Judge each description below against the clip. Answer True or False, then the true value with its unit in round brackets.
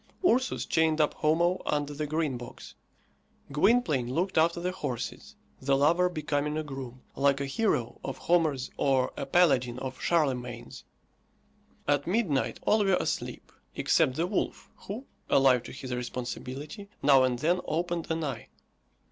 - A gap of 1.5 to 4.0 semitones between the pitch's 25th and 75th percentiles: False (4.6 semitones)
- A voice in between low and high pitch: True (145 Hz)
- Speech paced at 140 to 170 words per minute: True (150 wpm)